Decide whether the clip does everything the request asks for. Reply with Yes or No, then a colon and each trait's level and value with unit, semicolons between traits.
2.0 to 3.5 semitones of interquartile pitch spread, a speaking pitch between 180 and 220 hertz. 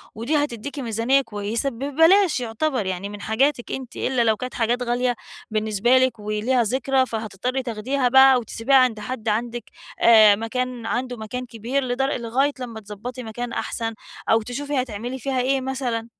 No: average, 2.8 semitones; high, 245 Hz